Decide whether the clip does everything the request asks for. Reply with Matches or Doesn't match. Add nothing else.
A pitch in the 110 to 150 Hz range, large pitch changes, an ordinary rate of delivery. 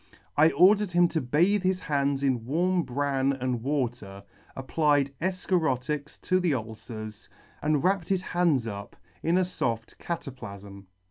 Matches